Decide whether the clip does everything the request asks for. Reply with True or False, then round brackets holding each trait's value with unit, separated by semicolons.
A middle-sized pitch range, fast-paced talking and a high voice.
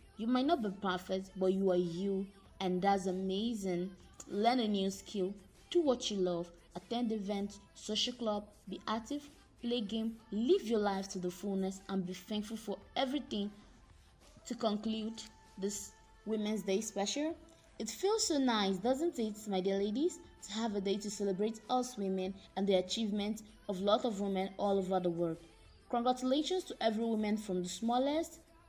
False (3.4 semitones; 165 wpm; 210 Hz)